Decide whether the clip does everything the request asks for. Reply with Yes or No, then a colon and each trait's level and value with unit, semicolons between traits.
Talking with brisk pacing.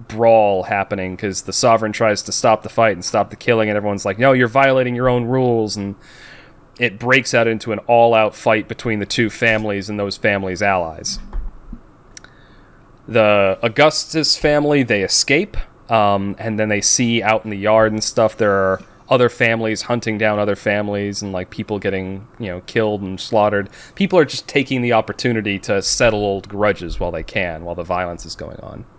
No: average, 190 wpm